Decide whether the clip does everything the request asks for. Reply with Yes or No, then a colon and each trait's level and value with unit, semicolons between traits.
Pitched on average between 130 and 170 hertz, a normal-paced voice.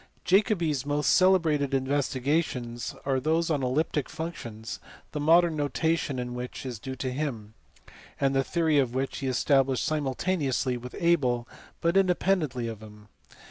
Yes: medium, 140 Hz; average, 145 wpm